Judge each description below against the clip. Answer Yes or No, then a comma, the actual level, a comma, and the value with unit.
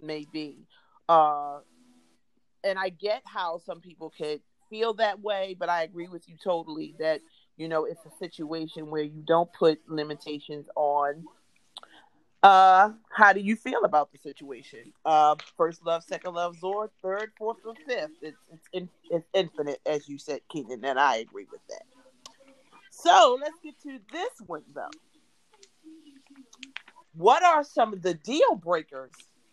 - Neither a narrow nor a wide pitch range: No, wide, 7.3 semitones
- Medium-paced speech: Yes, average, 155 wpm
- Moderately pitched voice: Yes, medium, 175 Hz